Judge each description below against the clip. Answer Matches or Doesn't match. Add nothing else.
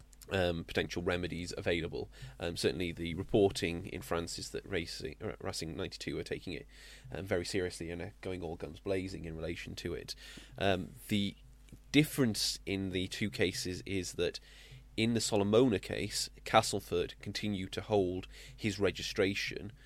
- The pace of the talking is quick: Doesn't match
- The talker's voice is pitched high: Doesn't match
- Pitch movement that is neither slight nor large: Matches